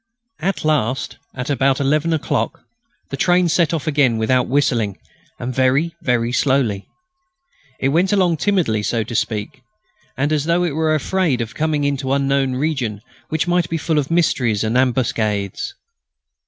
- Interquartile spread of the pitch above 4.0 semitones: Yes, average, 4.6 semitones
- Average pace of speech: Yes, average, 155 wpm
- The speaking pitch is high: No, medium, 140 Hz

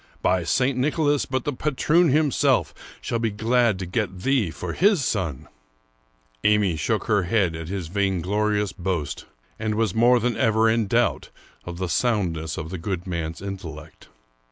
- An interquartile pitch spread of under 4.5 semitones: No, wide, 5.4 semitones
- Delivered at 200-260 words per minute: No, average, 170 wpm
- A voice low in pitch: Yes, low, 105 Hz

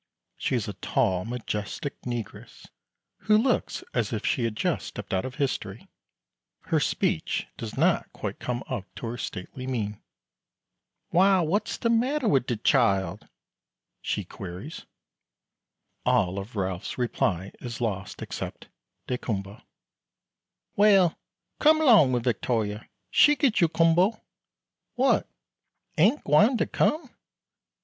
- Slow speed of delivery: Yes, slow, 125 wpm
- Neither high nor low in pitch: No, low, 125 Hz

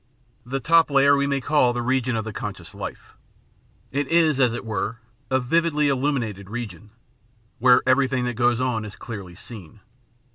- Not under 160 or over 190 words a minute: Yes, average, 170 wpm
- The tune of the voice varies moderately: Yes, average, 3.7 semitones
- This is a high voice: No, low, 125 Hz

